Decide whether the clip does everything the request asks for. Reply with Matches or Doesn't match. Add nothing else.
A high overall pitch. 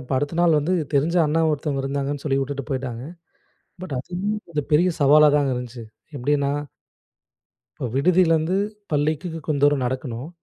Doesn't match